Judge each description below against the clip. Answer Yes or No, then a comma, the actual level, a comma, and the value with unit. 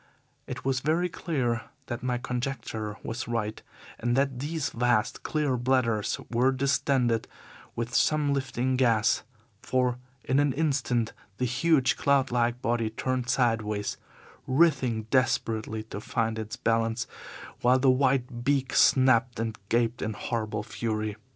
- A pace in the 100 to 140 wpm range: Yes, slow, 135 wpm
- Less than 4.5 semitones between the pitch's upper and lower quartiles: Yes, average, 2.7 semitones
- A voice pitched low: Yes, low, 125 Hz